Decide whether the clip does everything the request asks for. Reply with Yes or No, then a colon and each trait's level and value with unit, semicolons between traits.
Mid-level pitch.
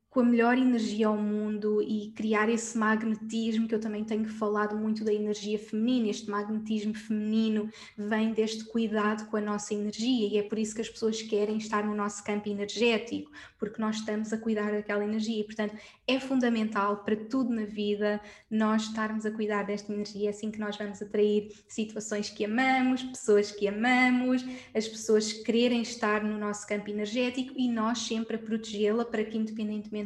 No: high, 215 Hz